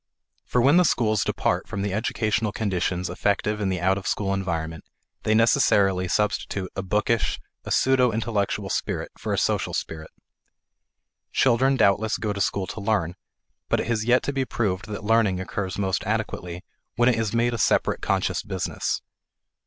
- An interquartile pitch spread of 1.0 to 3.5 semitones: Yes, average, 3.2 semitones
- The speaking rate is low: No, average, 170 wpm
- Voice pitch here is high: No, low, 105 Hz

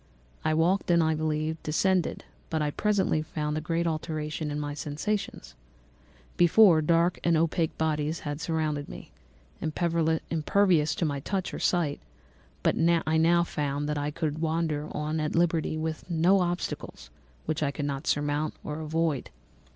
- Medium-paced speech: Yes, average, 160 wpm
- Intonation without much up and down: Yes, narrow, 1.9 semitones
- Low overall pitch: No, medium, 155 Hz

